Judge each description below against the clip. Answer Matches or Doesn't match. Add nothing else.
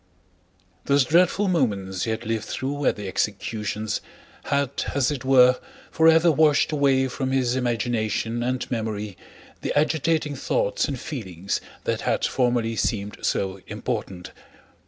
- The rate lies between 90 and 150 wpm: Matches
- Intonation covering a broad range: Doesn't match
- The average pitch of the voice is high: Doesn't match